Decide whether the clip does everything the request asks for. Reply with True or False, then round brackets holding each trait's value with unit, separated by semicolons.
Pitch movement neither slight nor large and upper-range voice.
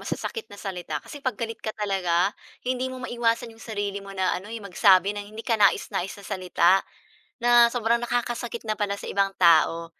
True (3.7 semitones; 210 Hz)